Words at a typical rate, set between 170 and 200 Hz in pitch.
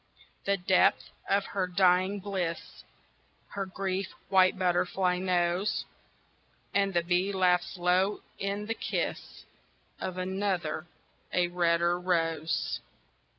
No: slow, 110 wpm; medium, 185 Hz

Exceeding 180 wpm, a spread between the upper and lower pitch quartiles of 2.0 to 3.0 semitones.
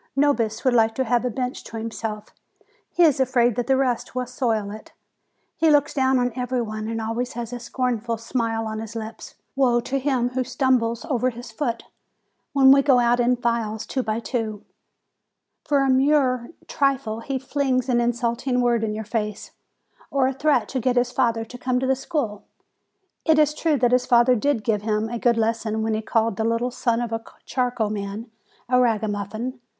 Yes: average, 195 wpm; narrow, 2.4 semitones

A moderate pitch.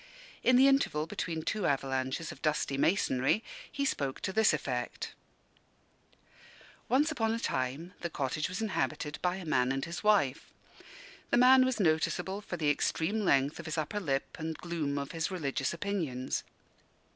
Yes: medium, 160 Hz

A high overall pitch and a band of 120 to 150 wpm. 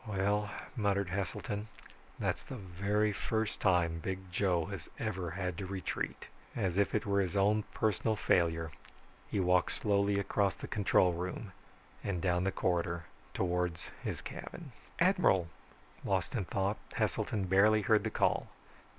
No: very low, 95 Hz; average, 145 wpm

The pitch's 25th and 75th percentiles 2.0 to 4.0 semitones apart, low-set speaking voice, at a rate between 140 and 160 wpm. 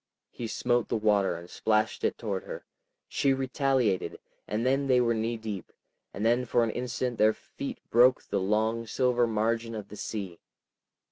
No: narrow, 2.6 semitones; low, 115 Hz; average, 175 wpm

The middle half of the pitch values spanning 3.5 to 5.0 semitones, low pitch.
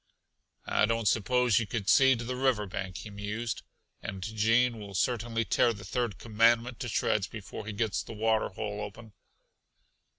No: narrow, 2.4 semitones; low, 110 Hz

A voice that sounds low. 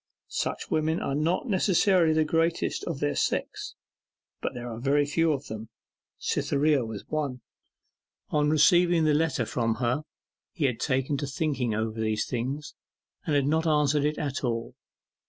No: medium, 145 Hz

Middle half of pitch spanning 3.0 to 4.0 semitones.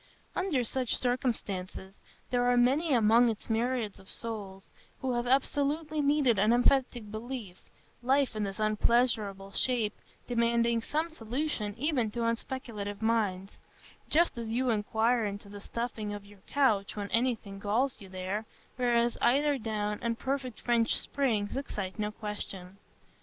Yes: average, 3.5 semitones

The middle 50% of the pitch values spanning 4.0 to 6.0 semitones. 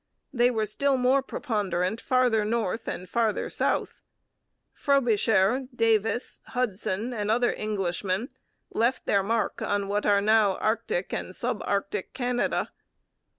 No: average, 3.4 semitones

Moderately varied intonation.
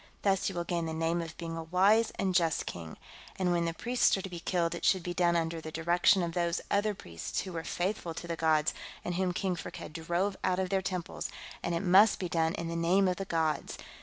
No: narrow, 2.3 semitones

